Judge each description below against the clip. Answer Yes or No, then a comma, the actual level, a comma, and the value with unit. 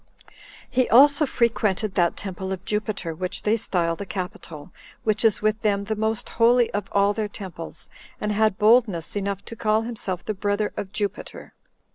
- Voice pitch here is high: Yes, high, 210 Hz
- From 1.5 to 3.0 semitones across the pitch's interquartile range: Yes, narrow, 2.5 semitones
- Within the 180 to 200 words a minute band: No, average, 170 wpm